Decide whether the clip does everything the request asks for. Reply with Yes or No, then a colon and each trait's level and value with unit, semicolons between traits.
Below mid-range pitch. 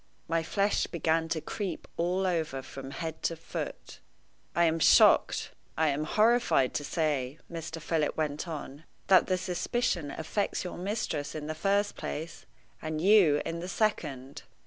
No: medium, 165 Hz